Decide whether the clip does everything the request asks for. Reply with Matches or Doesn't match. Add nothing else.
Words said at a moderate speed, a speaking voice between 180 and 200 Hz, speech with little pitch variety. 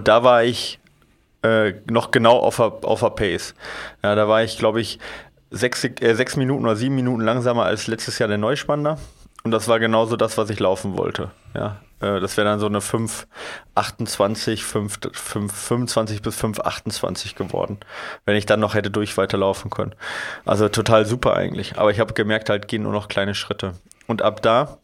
Doesn't match